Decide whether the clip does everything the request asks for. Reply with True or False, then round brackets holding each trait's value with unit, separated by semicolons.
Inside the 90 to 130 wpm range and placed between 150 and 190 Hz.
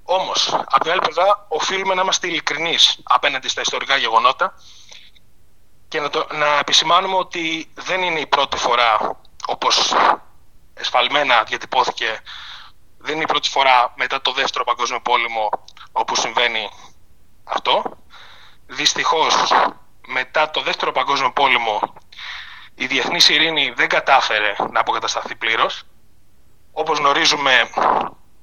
True (120 wpm; 185 Hz)